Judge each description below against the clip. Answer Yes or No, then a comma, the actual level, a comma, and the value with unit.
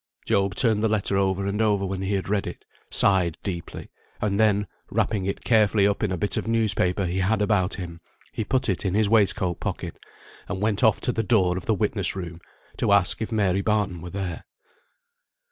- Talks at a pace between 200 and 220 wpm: Yes, fast, 205 wpm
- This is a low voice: Yes, low, 100 Hz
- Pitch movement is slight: Yes, narrow, 2.3 semitones